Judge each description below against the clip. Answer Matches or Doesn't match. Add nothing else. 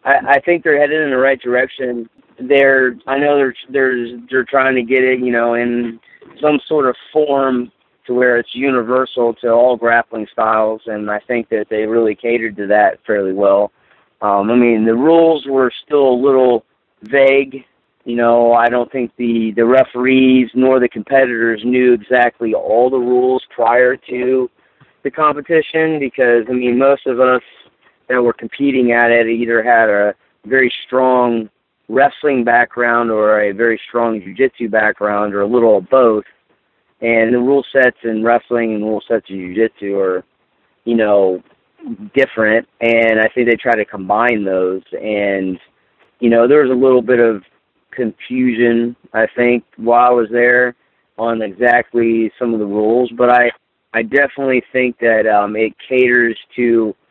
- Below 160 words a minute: Doesn't match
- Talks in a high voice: Doesn't match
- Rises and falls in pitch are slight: Matches